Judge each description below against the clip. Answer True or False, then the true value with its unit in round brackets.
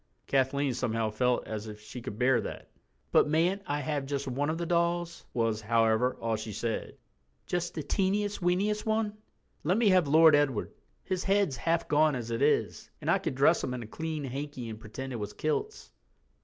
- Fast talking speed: False (195 wpm)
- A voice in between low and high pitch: True (145 Hz)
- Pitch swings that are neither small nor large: False (6.4 semitones)